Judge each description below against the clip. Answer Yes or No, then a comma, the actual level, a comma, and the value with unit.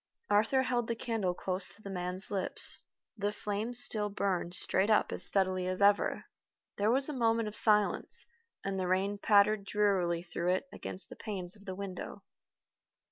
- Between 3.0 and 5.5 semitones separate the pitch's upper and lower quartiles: No, narrow, 2.5 semitones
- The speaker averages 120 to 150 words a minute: No, average, 175 wpm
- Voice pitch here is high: Yes, high, 200 Hz